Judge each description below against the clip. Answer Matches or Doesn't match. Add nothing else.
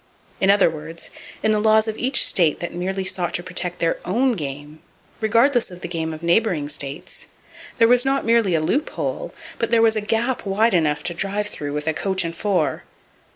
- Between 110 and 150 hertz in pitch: Doesn't match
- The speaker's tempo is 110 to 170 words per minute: Doesn't match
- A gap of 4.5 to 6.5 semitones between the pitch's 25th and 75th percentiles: Matches